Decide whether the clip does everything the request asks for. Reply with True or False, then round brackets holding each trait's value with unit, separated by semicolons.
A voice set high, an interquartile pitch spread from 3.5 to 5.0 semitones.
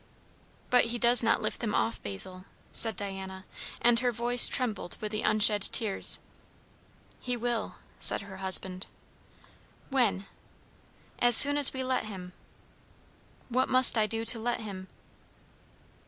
True (225 Hz; 3.9 semitones)